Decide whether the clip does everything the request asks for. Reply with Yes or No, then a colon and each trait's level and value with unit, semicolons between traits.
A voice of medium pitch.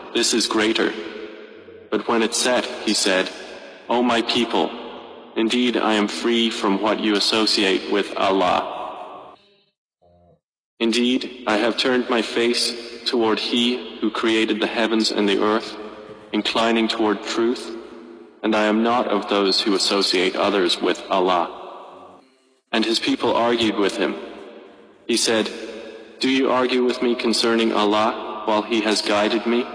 No: low, 110 Hz